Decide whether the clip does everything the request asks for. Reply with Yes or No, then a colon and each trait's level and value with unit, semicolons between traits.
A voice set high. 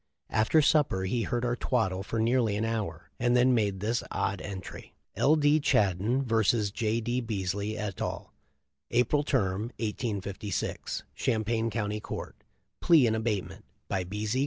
No: low, 110 Hz